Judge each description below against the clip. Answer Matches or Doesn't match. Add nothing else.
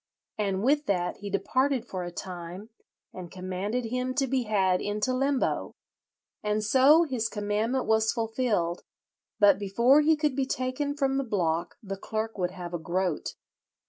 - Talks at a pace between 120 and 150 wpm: Doesn't match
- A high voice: Matches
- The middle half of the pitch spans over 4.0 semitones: Matches